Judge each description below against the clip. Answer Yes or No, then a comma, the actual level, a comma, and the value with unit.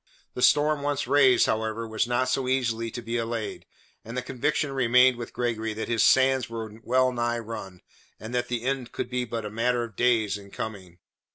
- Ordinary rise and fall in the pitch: No, narrow, 2.2 semitones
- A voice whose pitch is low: Yes, low, 120 Hz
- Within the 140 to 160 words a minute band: No, average, 200 wpm